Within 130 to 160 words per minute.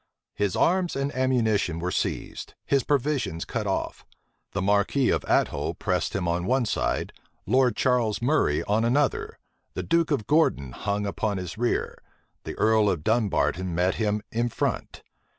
Yes: average, 155 wpm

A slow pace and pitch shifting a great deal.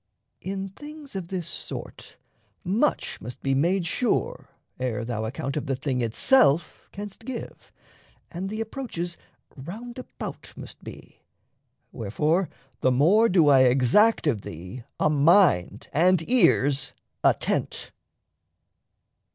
Yes: slow, 120 wpm; wide, 7.6 semitones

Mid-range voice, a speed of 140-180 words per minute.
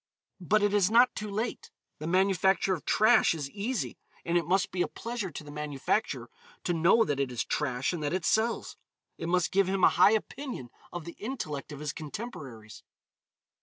No: medium, 180 Hz; average, 195 wpm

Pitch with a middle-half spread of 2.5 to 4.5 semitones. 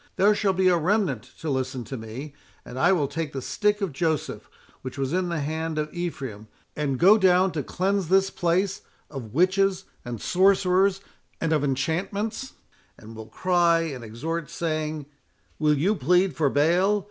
No: average, 5.2 semitones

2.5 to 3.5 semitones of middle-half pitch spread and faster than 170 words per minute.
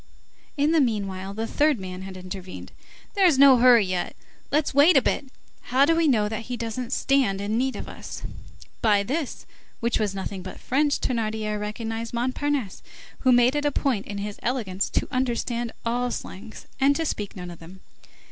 No: average, 5.0 semitones; average, 185 wpm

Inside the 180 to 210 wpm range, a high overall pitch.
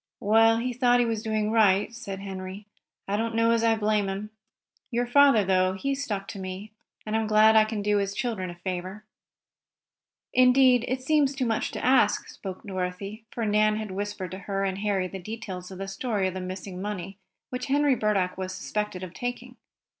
Yes: average, 200 wpm; high, 210 Hz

